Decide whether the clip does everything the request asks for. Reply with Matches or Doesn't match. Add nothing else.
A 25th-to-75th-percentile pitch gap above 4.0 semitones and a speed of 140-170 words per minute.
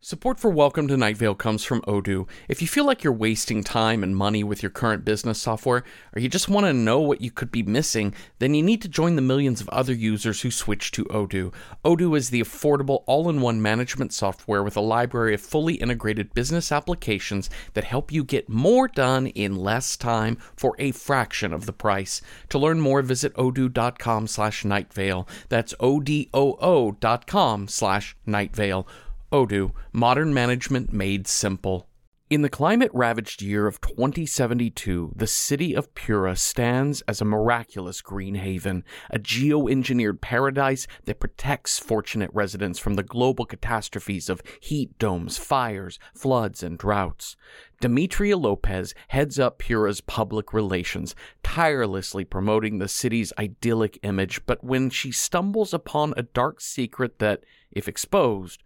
Matches